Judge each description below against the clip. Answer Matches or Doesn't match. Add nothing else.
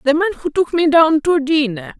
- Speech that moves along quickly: Matches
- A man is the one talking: Doesn't match